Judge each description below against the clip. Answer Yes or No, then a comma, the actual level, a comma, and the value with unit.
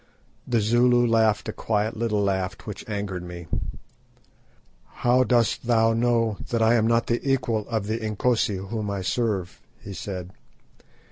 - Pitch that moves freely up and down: No, narrow, 2.6 semitones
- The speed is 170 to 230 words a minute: No, average, 150 wpm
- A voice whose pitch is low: Yes, low, 110 Hz